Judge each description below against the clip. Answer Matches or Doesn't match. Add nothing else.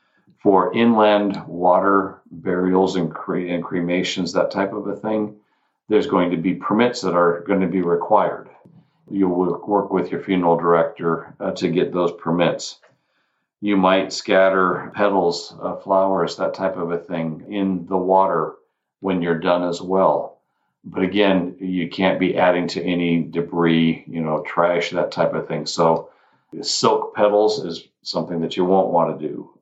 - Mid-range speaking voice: Doesn't match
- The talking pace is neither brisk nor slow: Matches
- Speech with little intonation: Matches